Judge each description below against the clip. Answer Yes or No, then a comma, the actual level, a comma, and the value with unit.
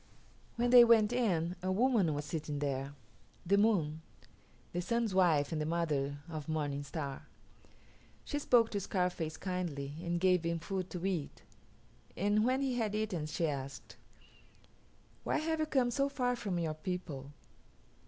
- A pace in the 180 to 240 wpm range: No, average, 155 wpm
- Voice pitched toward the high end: No, medium, 180 Hz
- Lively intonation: Yes, wide, 6.2 semitones